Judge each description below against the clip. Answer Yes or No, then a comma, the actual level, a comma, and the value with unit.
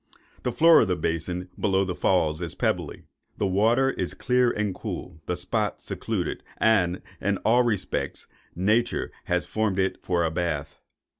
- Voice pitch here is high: No, very low, 95 Hz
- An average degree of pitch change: Yes, average, 4.1 semitones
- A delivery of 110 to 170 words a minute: Yes, average, 160 wpm